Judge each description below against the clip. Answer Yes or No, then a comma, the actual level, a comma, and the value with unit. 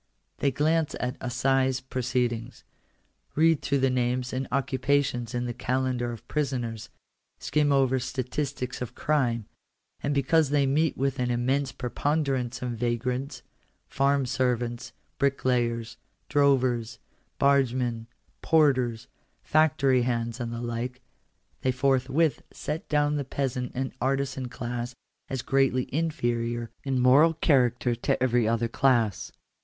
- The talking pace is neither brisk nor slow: No, slow, 125 wpm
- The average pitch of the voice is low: Yes, low, 130 Hz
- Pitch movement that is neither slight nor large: No, narrow, 2.3 semitones